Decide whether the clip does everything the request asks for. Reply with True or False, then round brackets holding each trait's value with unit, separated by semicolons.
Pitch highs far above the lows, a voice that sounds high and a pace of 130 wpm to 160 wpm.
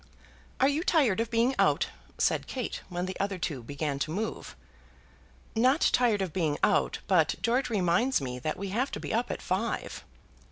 False (6.4 semitones; 205 Hz; 185 wpm)